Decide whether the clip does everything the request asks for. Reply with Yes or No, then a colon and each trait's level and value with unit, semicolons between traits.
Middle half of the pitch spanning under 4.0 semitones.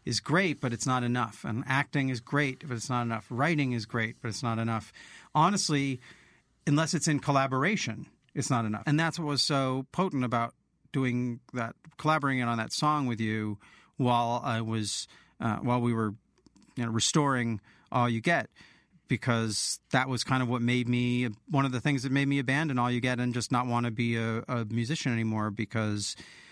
Yes: average, 3.1 semitones